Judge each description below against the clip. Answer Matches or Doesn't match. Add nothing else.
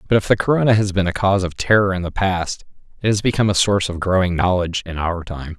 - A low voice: Matches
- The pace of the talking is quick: Matches